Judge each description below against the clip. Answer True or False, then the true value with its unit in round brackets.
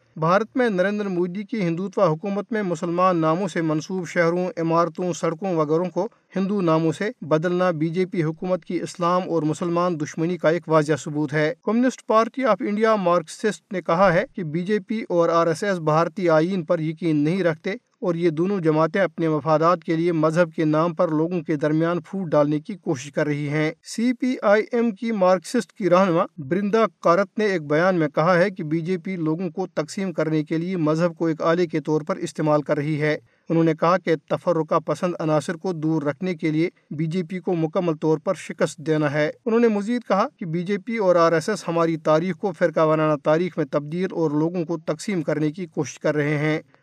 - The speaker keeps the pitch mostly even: False (3.1 semitones)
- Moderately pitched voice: True (170 Hz)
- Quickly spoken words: True (215 wpm)